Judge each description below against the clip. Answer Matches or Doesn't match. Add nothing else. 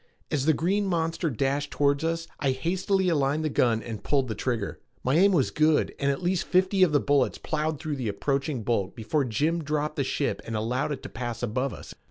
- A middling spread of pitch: Matches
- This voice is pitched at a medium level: Matches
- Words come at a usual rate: Doesn't match